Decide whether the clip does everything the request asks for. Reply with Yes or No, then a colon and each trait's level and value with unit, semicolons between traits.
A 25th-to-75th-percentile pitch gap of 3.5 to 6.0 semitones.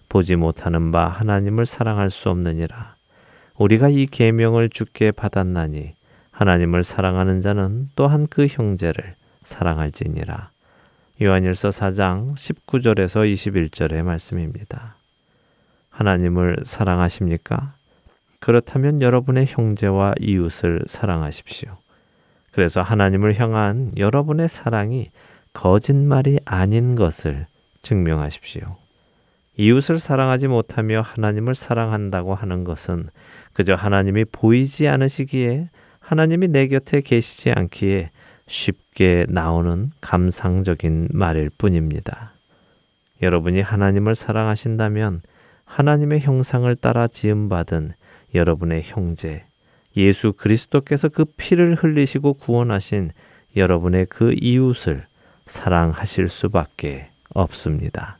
Yes: wide, 5.6 semitones